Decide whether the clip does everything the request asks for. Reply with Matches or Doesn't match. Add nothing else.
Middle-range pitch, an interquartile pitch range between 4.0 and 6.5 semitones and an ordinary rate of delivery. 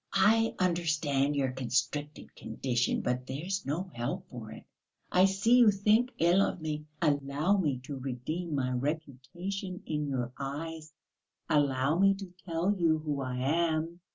Matches